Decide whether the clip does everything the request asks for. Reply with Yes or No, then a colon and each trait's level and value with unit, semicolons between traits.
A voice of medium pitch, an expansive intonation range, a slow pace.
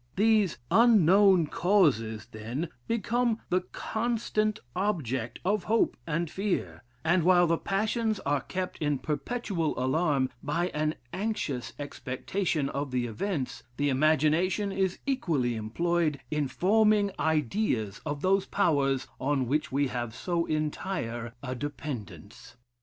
Yes: medium, 160 Hz; wide, 6.2 semitones; slow, 125 wpm